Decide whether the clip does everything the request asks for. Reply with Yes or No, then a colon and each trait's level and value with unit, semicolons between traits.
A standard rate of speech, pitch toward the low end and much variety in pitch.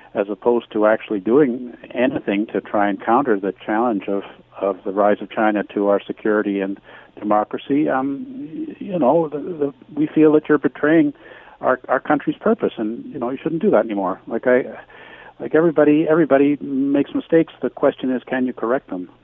Yes: average, 185 wpm; low, 130 Hz; wide, 7.2 semitones